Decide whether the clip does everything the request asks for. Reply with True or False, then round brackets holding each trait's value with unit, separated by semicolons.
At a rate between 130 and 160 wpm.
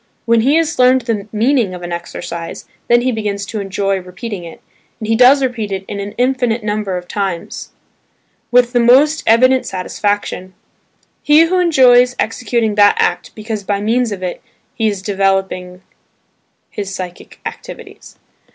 True (150 wpm)